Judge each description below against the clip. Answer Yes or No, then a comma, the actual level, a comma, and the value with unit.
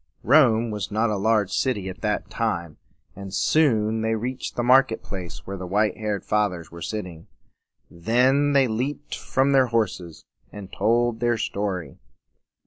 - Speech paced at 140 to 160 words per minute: Yes, average, 155 wpm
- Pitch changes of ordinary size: Yes, average, 3.7 semitones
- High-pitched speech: No, low, 110 Hz